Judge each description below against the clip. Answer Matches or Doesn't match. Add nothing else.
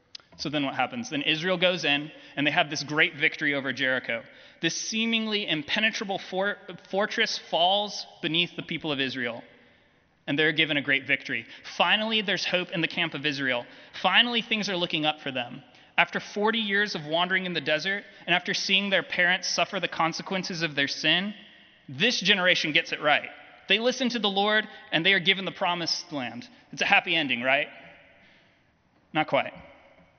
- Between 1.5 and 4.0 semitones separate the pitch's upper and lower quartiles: Doesn't match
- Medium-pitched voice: Matches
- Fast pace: Doesn't match